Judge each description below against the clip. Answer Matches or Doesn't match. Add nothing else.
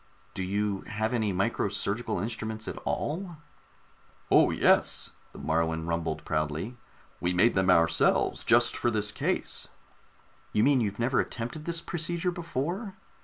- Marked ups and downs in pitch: Matches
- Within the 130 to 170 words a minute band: Matches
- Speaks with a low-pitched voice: Matches